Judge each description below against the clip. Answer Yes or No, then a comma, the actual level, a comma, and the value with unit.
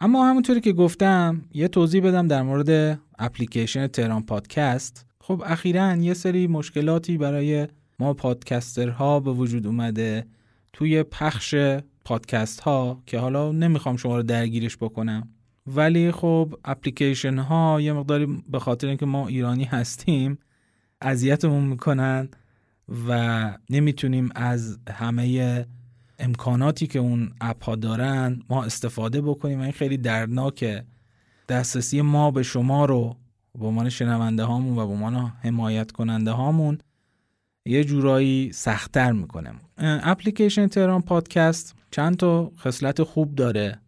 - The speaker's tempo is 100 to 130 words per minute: Yes, average, 125 wpm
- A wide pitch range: No, average, 4.2 semitones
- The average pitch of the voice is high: No, low, 130 Hz